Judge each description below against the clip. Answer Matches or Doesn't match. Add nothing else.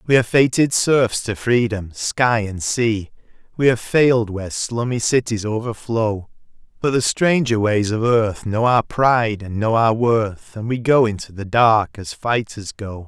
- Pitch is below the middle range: Matches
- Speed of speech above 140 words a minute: Matches